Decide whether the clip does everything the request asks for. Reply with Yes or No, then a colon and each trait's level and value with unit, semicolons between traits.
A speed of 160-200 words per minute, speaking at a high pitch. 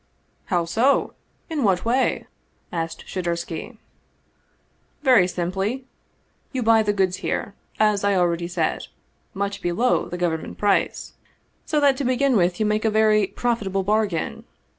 No: average, 150 wpm; high, 205 Hz